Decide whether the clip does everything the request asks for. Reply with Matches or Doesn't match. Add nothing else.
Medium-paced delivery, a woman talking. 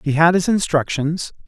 Doesn't match